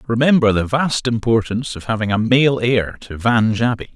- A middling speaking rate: Yes, average, 180 wpm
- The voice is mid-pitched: No, low, 115 Hz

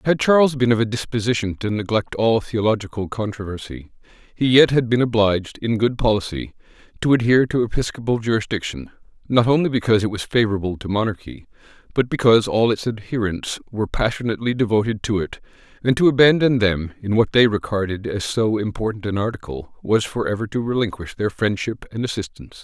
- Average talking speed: Yes, average, 165 wpm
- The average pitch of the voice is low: Yes, low, 110 Hz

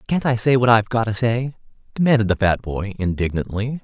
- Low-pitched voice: Yes, low, 115 Hz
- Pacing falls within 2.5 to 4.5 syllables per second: No, 5.9 syllables/s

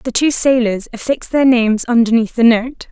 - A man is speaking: No, female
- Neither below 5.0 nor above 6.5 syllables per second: Yes, 5.3 syllables/s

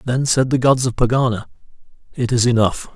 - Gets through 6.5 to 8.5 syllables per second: No, 5.6 syllables/s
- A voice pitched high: No, low, 120 Hz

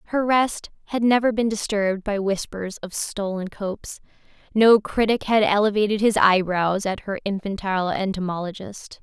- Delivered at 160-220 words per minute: No, average, 140 wpm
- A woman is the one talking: Yes, female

